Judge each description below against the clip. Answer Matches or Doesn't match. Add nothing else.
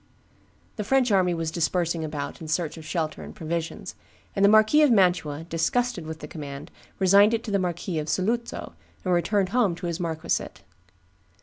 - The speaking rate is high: Doesn't match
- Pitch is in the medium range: Matches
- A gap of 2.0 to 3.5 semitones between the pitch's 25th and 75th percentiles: Doesn't match